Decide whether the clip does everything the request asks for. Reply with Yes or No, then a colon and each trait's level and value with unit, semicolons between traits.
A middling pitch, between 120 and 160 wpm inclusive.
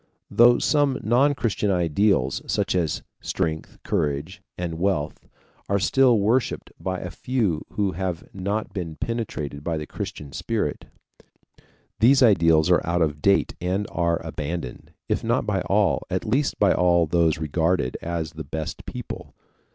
No: very low, 90 Hz; average, 150 wpm